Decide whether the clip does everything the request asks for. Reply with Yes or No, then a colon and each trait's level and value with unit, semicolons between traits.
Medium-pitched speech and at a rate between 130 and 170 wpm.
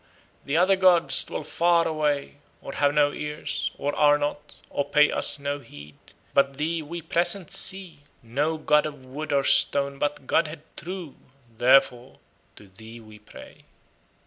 Yes: medium, 145 Hz; average, 155 wpm